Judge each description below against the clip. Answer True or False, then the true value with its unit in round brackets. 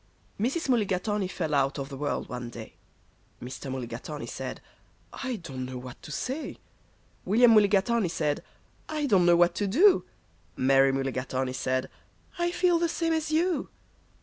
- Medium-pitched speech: True (175 Hz)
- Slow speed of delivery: False (150 wpm)